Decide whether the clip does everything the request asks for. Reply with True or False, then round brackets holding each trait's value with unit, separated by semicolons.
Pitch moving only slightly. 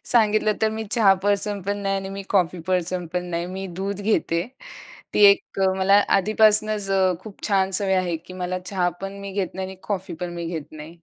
True (2.2 semitones)